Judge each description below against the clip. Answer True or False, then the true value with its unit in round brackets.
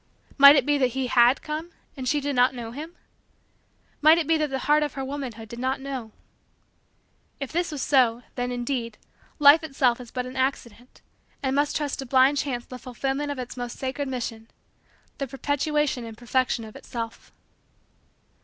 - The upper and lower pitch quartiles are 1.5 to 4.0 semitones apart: True (2.8 semitones)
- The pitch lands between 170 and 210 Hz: False (265 Hz)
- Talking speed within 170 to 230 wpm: True (180 wpm)